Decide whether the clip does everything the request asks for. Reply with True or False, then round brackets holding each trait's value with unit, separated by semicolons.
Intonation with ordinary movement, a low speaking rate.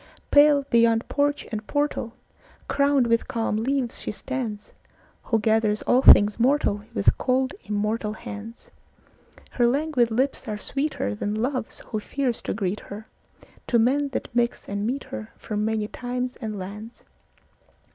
True (3.9 semitones; 125 wpm)